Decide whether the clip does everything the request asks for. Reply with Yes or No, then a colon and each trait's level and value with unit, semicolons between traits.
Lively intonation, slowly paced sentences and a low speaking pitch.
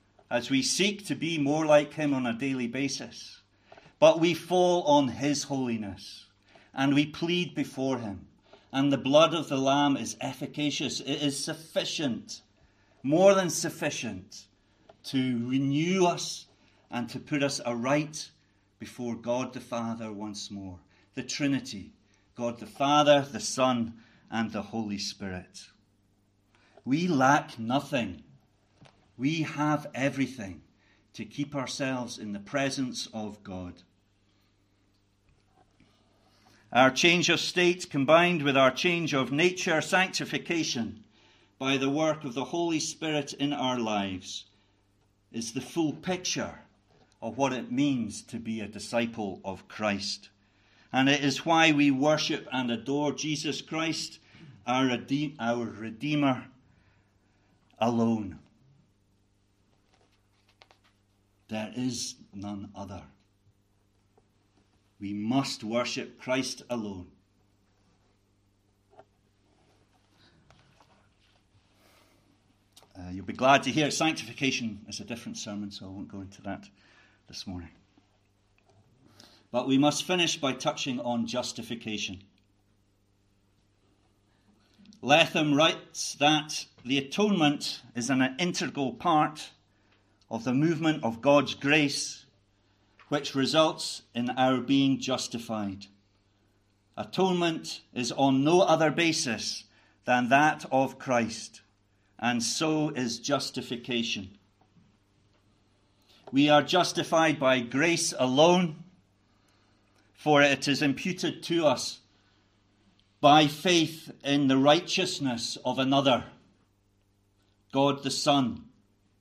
Yes: wide, 6.2 semitones; slow, 110 wpm; low, 120 Hz